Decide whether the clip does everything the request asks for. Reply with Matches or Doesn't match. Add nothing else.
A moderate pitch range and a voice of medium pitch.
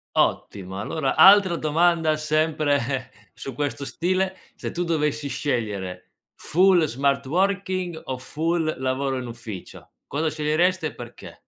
Matches